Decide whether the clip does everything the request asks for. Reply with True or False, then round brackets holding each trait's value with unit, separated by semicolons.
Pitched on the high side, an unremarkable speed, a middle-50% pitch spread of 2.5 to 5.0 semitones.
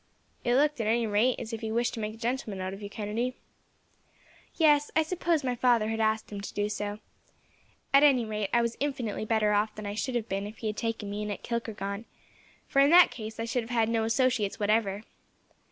False (225 Hz; 225 wpm; 2.8 semitones)